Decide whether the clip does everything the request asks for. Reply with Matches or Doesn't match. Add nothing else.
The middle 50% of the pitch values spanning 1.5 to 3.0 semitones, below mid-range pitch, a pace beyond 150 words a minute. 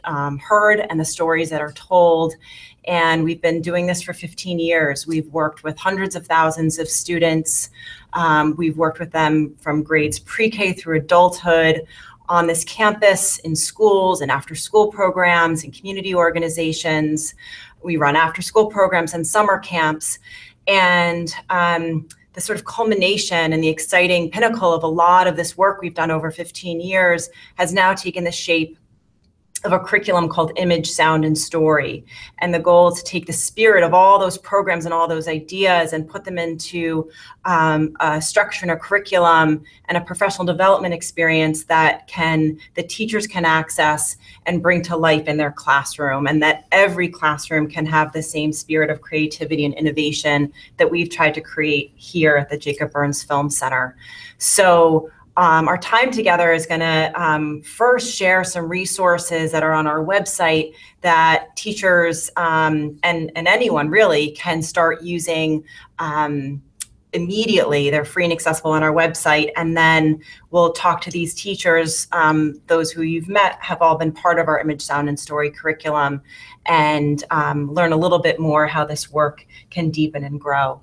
Doesn't match